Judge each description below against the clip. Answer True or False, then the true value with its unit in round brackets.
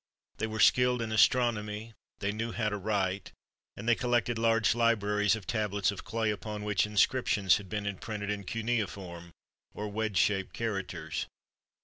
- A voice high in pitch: False (105 Hz)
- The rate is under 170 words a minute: True (160 wpm)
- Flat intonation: True (2.0 semitones)